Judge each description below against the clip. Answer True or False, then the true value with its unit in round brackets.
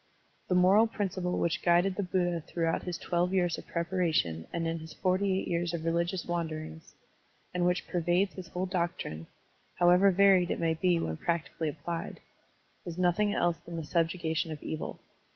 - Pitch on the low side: False (175 Hz)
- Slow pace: False (170 wpm)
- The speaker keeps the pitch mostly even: True (1.8 semitones)